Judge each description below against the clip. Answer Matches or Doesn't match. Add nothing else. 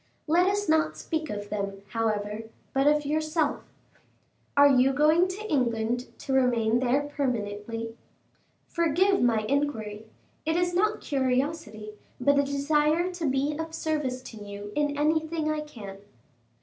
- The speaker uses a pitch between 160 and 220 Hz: Doesn't match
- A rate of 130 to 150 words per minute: Matches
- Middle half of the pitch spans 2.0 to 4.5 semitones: Doesn't match